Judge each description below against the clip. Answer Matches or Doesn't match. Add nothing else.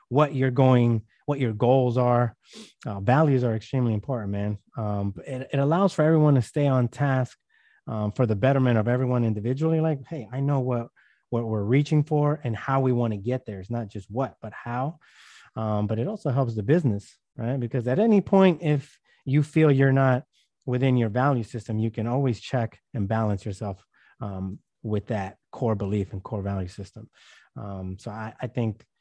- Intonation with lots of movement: Doesn't match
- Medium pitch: Doesn't match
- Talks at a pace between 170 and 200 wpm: Matches